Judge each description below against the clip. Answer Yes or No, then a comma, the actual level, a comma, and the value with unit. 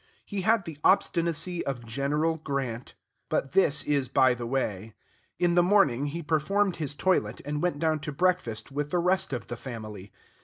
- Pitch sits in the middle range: Yes, medium, 145 Hz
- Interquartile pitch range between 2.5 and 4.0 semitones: No, wide, 5.4 semitones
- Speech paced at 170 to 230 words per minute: Yes, average, 180 wpm